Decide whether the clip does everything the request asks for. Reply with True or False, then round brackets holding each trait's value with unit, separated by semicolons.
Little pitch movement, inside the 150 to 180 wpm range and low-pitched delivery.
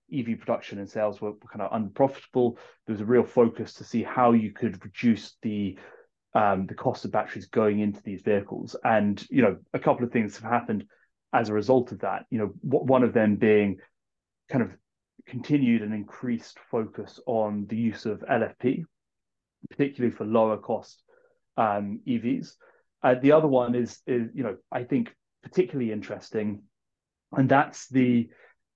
False (3.4 semitones; 170 wpm; 115 Hz)